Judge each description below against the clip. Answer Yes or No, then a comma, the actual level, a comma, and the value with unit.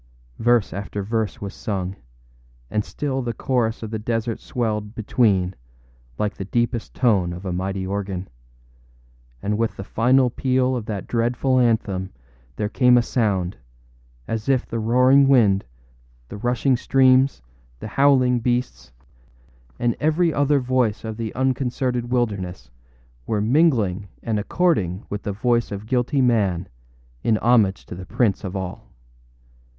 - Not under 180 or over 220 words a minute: No, average, 145 wpm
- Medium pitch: No, low, 115 Hz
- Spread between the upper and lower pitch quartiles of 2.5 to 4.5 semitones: Yes, average, 3.9 semitones